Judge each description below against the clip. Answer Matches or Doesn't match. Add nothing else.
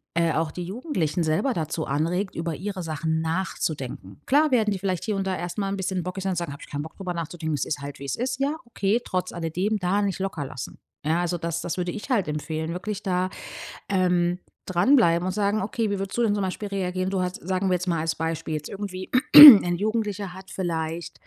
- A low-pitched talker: Doesn't match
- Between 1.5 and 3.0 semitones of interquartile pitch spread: Doesn't match